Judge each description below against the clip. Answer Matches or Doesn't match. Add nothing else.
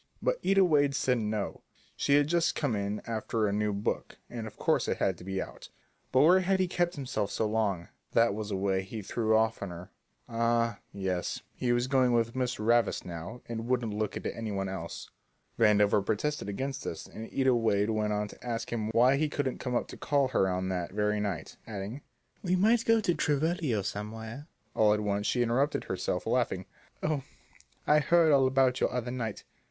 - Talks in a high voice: Doesn't match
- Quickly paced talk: Matches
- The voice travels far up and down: Doesn't match